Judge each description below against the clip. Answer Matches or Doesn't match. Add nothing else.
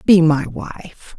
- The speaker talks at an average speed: Matches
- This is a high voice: Doesn't match